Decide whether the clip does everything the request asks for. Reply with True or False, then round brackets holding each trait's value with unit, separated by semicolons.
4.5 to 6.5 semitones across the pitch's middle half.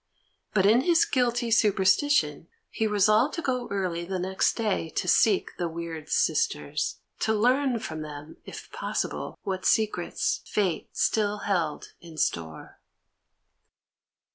True (5.2 semitones)